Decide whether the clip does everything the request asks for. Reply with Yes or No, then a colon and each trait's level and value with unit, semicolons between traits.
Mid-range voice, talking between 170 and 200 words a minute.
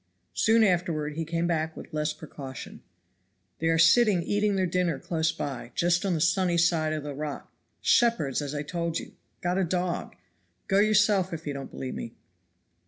Yes: medium, 170 Hz; average, 180 wpm